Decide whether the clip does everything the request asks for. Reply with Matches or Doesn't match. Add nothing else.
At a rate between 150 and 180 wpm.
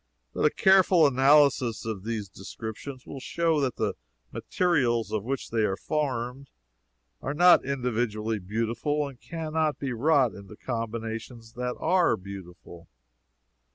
Doesn't match